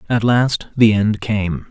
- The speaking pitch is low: Yes, low, 110 Hz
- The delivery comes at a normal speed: Yes, average, 175 wpm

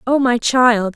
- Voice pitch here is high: Yes, high, 240 Hz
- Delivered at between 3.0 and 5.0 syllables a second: Yes, 3.5 syllables/s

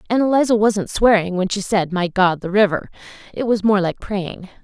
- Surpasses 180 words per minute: Yes, fast, 205 wpm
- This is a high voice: Yes, high, 200 Hz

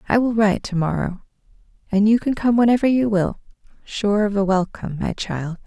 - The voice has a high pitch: Yes, high, 205 Hz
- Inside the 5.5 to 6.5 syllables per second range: Yes, 5.6 syllables/s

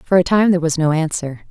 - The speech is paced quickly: Yes, fast, 280 wpm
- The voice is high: No, medium, 170 Hz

